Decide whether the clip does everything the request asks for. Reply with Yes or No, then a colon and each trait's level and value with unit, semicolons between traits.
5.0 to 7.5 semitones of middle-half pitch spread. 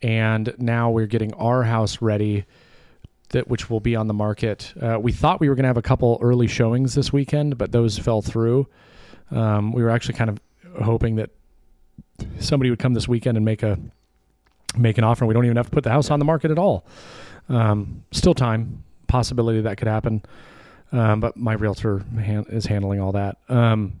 No: narrow, 2.4 semitones